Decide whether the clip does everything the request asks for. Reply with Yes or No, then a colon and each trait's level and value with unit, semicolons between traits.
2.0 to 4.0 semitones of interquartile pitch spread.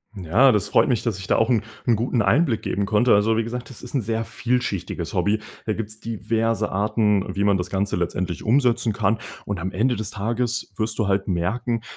Yes: average, 2.8 semitones